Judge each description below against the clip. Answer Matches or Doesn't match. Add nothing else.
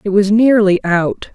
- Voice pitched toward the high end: Matches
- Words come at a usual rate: Matches